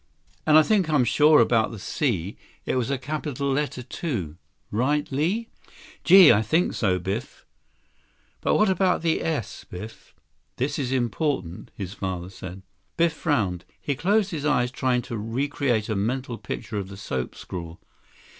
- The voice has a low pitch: Yes, low, 125 Hz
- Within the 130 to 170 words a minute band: Yes, average, 160 wpm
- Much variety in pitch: Yes, wide, 6.8 semitones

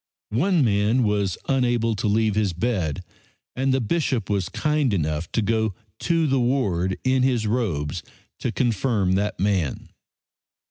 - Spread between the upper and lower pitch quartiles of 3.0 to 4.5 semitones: No, average, 4.9 semitones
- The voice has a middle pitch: No, low, 110 Hz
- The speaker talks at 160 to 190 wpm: No, average, 145 wpm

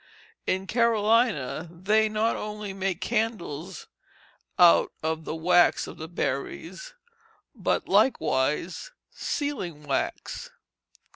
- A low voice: No, high, 190 Hz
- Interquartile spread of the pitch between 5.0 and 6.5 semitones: Yes, average, 5.3 semitones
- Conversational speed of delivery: No, slow, 95 wpm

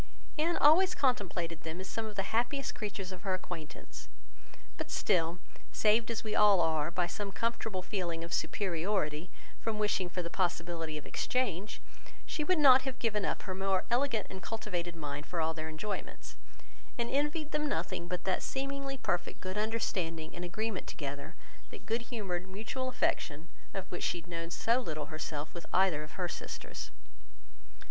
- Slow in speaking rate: No, average, 175 wpm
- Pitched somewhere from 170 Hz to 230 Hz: Yes, high, 190 Hz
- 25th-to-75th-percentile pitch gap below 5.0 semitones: No, average, 5.3 semitones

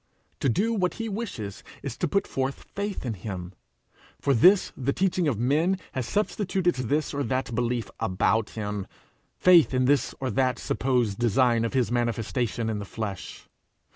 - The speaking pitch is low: Yes, low, 130 Hz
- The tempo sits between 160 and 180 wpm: Yes, average, 170 wpm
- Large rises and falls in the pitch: Yes, wide, 6.8 semitones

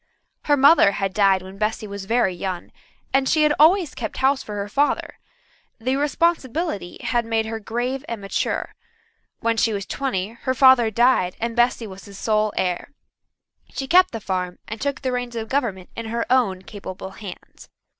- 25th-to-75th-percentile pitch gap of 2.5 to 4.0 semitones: No, average, 4.8 semitones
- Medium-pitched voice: No, high, 225 Hz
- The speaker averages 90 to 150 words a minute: No, average, 175 wpm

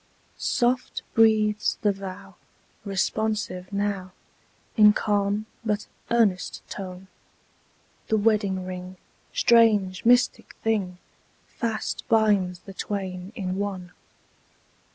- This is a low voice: No, high, 205 Hz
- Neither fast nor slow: No, slow, 90 wpm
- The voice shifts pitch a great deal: No, average, 2.7 semitones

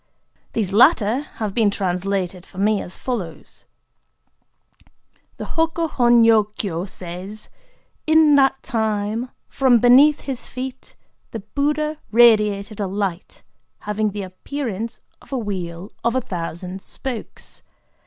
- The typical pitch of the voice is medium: No, high, 215 Hz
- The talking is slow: Yes, slow, 125 wpm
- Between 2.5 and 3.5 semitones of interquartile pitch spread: No, average, 4.8 semitones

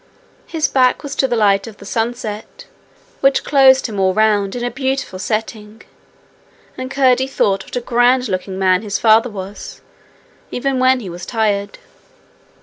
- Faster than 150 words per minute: Yes, average, 160 wpm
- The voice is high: Yes, high, 225 Hz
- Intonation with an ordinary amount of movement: Yes, average, 4.3 semitones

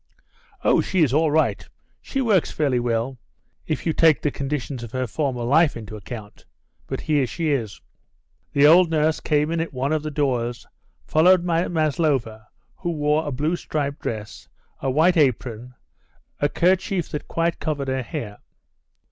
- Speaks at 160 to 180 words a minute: Yes, average, 165 wpm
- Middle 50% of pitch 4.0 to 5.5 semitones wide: Yes, average, 4.3 semitones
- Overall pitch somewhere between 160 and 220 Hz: No, medium, 145 Hz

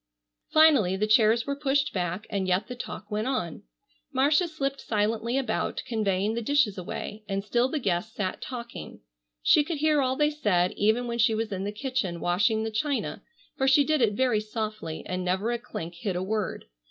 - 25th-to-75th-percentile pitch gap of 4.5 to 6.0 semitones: Yes, average, 4.9 semitones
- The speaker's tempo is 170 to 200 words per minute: Yes, average, 195 wpm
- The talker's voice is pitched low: No, high, 220 Hz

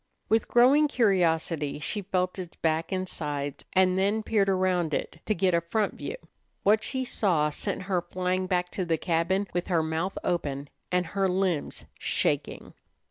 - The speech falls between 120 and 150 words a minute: No, average, 170 wpm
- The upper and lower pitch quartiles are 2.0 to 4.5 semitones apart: Yes, average, 2.9 semitones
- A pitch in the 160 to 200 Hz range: Yes, medium, 185 Hz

